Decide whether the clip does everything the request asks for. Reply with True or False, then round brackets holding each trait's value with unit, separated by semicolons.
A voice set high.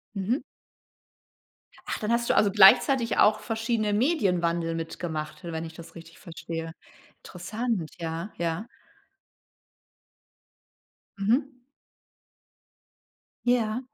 True (195 Hz)